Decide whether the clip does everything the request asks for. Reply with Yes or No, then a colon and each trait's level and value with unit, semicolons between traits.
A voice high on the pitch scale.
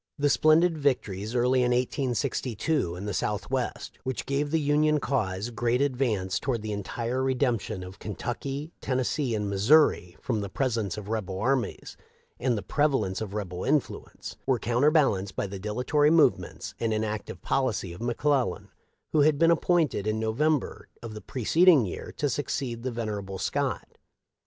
No: low, 120 Hz